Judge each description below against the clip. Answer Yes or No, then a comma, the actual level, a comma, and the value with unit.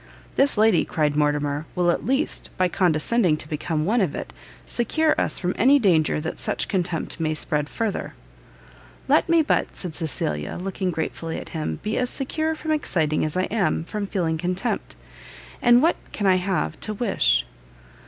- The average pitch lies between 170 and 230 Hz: Yes, medium, 185 Hz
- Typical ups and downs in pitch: No, wide, 6.4 semitones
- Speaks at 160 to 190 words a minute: Yes, average, 175 wpm